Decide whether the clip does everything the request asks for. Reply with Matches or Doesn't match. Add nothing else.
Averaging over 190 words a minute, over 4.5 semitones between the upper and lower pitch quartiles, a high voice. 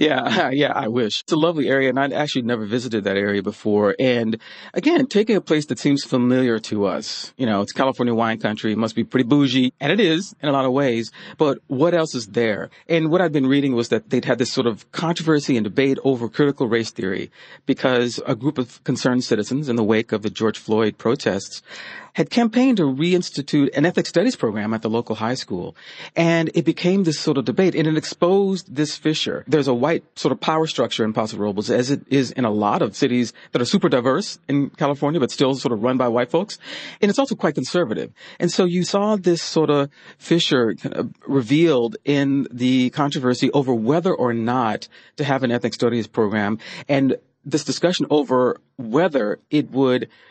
Doesn't match